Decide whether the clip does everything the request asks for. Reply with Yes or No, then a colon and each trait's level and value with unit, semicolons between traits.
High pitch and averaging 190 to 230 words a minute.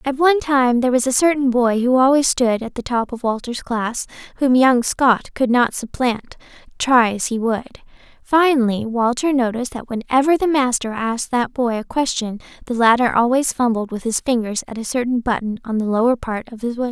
Yes: high, 245 Hz; average, 200 wpm